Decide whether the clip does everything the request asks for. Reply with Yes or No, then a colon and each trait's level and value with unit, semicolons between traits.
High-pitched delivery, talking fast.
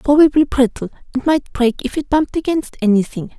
No: very high, 265 Hz; average, 195 wpm